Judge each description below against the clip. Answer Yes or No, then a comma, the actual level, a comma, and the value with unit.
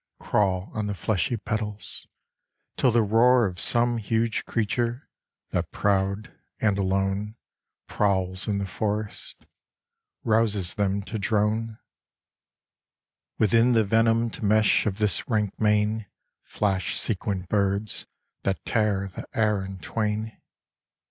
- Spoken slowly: Yes, slow, 115 wpm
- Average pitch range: No, narrow, 2.2 semitones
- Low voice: Yes, low, 105 Hz